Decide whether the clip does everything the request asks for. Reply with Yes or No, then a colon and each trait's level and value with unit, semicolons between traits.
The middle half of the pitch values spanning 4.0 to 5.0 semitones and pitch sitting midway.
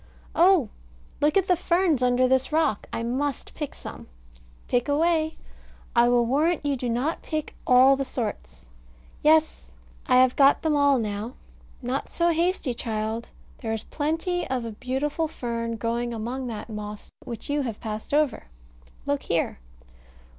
No: average, 4.7 semitones; very high, 260 Hz